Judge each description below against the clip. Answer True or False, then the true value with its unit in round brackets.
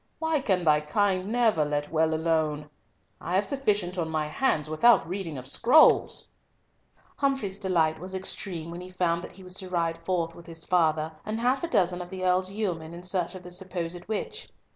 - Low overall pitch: False (180 Hz)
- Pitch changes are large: False (3.2 semitones)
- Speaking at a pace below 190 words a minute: False (195 wpm)